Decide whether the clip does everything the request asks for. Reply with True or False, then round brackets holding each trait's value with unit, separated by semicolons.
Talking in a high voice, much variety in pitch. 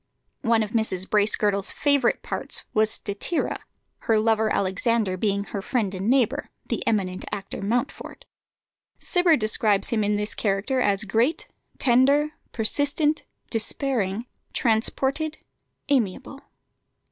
False (220 Hz; 4.5 semitones)